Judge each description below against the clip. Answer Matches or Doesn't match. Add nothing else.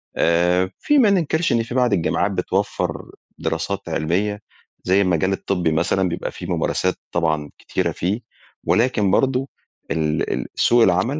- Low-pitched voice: Matches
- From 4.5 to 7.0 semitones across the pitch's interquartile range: Matches